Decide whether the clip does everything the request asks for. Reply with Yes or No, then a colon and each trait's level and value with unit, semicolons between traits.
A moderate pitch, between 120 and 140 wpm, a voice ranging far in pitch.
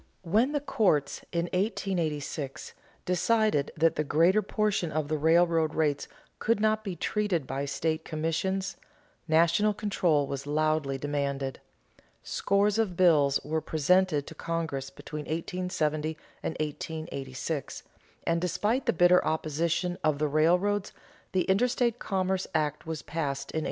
No: medium, 165 Hz; slow, 135 wpm; average, 4.0 semitones